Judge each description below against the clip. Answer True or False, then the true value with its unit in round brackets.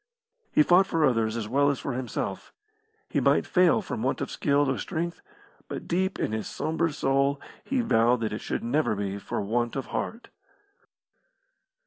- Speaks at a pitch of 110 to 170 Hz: True (135 Hz)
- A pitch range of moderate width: False (6.2 semitones)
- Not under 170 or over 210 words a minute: True (175 wpm)